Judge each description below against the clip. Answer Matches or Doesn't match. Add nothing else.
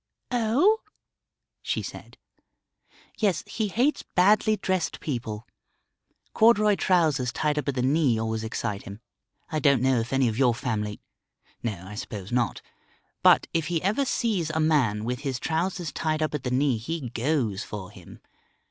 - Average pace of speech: Matches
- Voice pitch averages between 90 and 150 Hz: Matches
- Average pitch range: Doesn't match